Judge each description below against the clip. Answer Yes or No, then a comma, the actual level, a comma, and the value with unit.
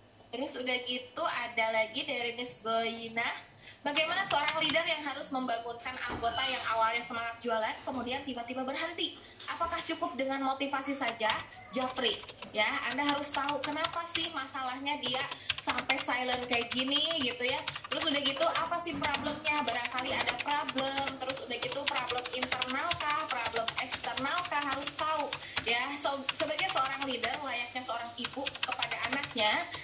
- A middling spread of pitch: Yes, average, 3.4 semitones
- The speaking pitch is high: Yes, very high, 270 Hz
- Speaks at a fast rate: Yes, fast, 145 wpm